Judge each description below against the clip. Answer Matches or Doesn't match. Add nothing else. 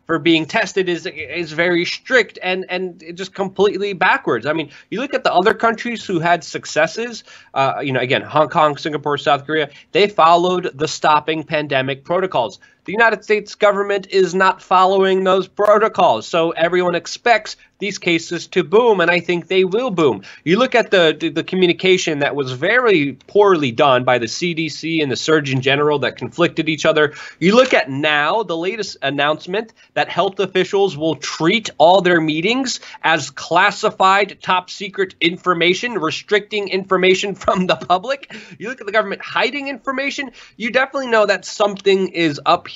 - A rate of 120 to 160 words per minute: Doesn't match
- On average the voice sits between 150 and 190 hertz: Matches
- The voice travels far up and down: Doesn't match